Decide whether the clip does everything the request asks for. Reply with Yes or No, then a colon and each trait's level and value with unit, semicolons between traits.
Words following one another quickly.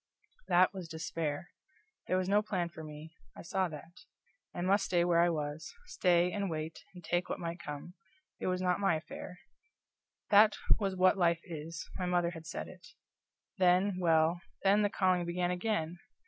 No: average, 175 wpm